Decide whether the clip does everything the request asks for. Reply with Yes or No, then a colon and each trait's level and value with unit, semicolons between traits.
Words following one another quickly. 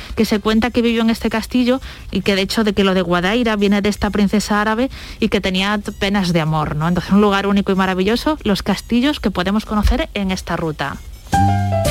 Yes: fast, 220 wpm